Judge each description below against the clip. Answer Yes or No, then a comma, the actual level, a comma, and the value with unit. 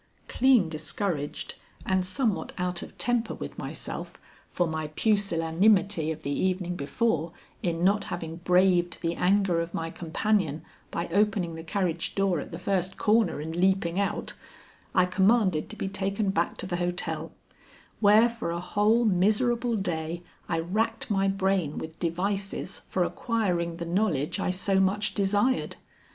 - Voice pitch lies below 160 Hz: No, medium, 185 Hz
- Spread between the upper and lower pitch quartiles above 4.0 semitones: No, average, 3.4 semitones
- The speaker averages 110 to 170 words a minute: Yes, average, 150 wpm